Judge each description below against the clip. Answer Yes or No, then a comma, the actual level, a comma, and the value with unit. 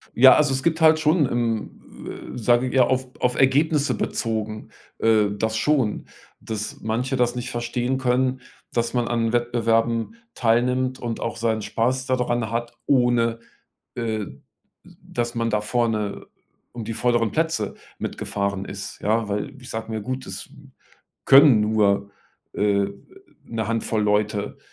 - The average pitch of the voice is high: No, low, 120 Hz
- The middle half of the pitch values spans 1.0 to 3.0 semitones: Yes, narrow, 2.6 semitones